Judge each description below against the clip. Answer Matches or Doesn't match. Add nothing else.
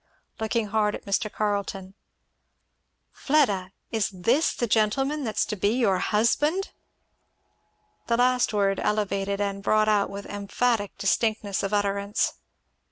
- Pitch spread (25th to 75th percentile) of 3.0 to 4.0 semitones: Doesn't match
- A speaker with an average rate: Doesn't match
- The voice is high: Matches